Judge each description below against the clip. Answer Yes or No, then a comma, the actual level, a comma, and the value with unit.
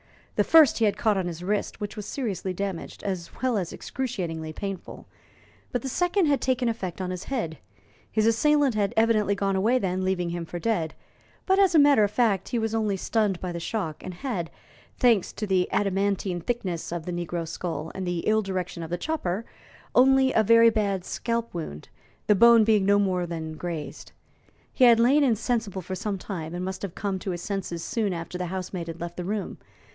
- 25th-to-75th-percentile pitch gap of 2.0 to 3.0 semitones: No, average, 4.6 semitones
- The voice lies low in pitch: No, high, 195 Hz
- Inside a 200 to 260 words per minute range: Yes, fast, 205 wpm